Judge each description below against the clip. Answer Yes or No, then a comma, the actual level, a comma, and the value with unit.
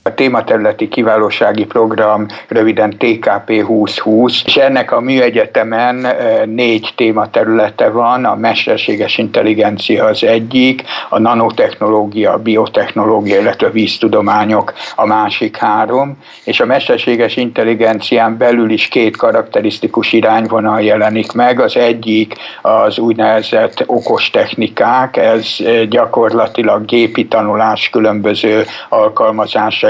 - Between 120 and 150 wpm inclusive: No, slow, 105 wpm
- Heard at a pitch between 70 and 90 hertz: No, low, 115 Hz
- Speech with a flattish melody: Yes, narrow, 1.9 semitones